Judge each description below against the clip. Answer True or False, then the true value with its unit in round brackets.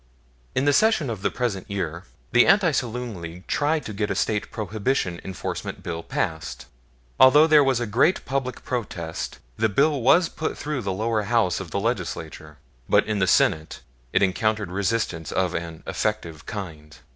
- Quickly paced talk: False (170 wpm)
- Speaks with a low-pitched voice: True (105 Hz)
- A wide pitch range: True (6.2 semitones)